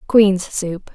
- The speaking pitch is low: No, high, 190 Hz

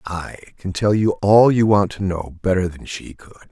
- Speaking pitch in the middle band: No, very low, 95 Hz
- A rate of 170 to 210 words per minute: No, fast, 220 wpm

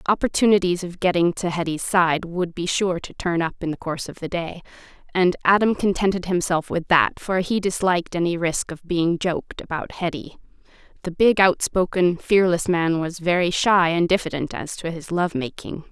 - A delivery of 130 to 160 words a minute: No, average, 180 wpm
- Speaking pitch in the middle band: Yes, medium, 175 Hz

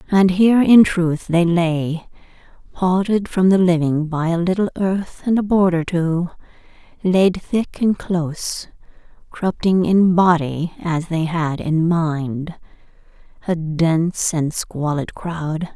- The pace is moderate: No, slow, 125 wpm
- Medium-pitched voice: Yes, medium, 175 Hz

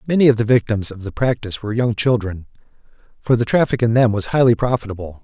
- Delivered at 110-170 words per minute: No, fast, 205 wpm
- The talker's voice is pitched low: Yes, low, 115 Hz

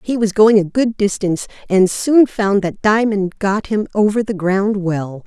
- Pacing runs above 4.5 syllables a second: No, 4.4 syllables/s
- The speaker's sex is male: No, female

